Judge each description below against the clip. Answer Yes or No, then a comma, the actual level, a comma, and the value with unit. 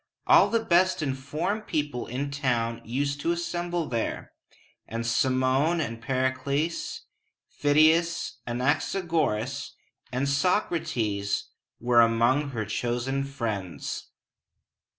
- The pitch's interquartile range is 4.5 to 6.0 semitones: Yes, average, 5.0 semitones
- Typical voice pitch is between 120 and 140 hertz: Yes, low, 135 Hz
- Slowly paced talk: Yes, slow, 100 wpm